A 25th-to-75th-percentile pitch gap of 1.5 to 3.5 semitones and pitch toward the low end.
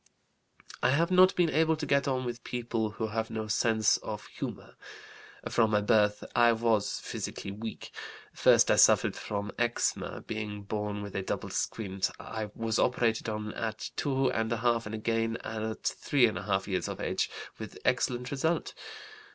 Yes: narrow, 2.5 semitones; low, 110 Hz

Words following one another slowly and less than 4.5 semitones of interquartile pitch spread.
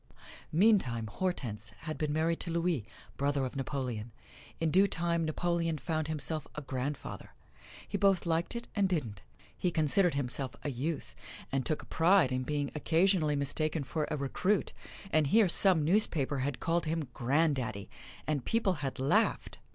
No: average, 160 wpm; average, 3.9 semitones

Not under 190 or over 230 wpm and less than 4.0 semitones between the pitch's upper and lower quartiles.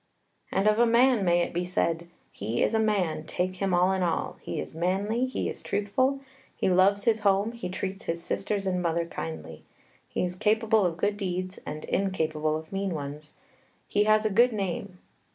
Yes: average, 195 wpm; average, 3.6 semitones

